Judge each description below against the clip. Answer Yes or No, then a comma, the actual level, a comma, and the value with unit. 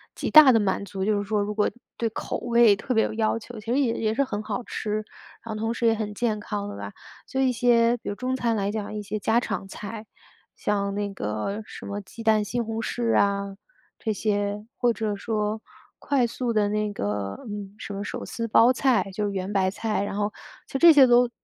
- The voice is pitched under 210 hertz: No, high, 215 Hz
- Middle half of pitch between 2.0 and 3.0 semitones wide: Yes, narrow, 2.4 semitones